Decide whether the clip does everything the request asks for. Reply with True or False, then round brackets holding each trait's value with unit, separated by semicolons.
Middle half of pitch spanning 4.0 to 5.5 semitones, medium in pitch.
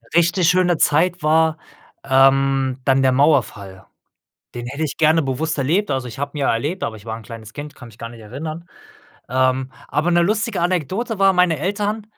True (5.2 semitones; 145 Hz)